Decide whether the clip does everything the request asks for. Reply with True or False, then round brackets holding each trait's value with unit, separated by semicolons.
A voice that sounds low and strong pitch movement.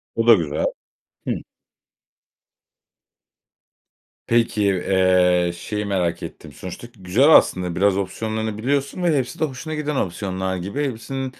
True (105 Hz; 6.1 semitones)